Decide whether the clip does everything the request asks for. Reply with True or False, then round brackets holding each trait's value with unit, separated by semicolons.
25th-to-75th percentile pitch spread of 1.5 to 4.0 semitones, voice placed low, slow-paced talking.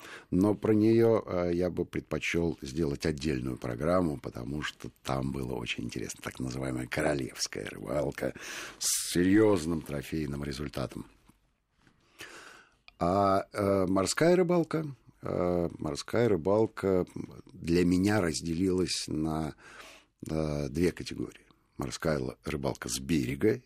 False (5.4 semitones; 85 Hz; 95 wpm)